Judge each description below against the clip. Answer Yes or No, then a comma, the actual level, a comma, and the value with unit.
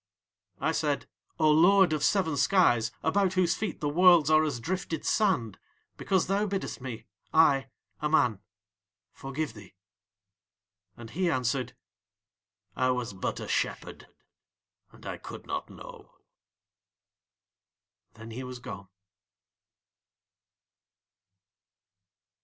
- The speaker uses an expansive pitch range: Yes, wide, 6.6 semitones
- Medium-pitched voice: Yes, medium, 150 Hz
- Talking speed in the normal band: No, slow, 115 wpm